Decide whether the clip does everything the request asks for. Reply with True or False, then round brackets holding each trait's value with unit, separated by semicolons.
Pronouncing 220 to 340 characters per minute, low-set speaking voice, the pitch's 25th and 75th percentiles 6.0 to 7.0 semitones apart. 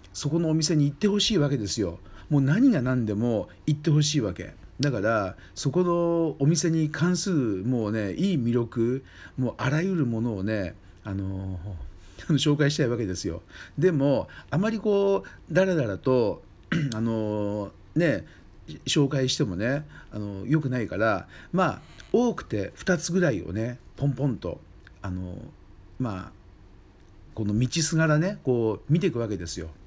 False (295 characters per minute; 125 Hz; 7.8 semitones)